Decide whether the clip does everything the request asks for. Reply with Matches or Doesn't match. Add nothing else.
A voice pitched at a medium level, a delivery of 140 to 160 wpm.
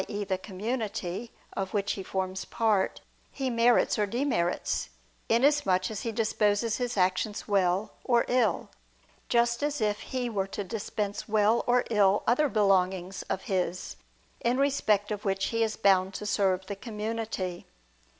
Doesn't match